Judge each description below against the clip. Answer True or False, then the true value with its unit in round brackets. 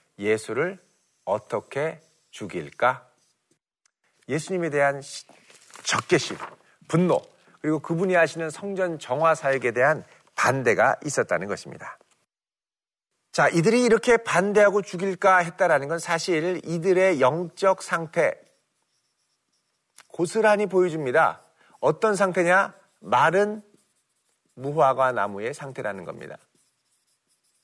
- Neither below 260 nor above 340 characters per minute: False (230 characters per minute)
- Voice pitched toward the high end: False (175 Hz)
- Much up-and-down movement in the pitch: False (4.0 semitones)